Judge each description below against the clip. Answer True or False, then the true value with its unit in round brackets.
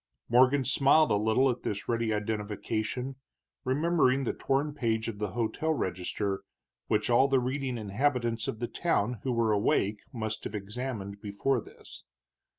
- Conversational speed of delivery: True (155 wpm)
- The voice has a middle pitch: False (115 Hz)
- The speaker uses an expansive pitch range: False (4.0 semitones)